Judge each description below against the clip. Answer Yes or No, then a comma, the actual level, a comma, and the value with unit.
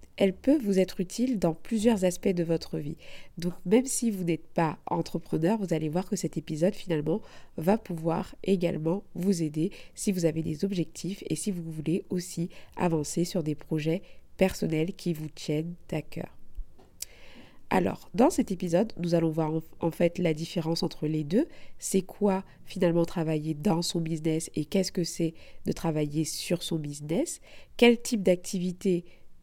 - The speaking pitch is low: No, medium, 175 Hz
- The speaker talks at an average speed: Yes, average, 170 wpm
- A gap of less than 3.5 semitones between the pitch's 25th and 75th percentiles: Yes, average, 2.9 semitones